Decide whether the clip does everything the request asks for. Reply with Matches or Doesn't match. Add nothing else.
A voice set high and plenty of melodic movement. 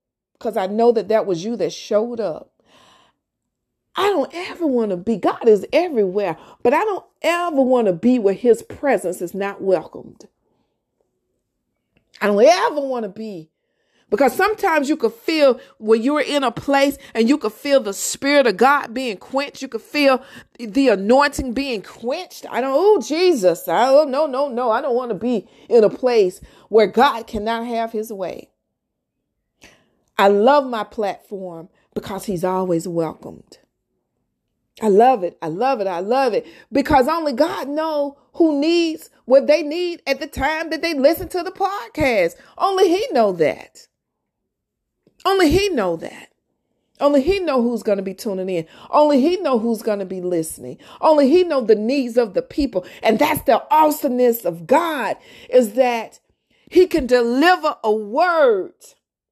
Matches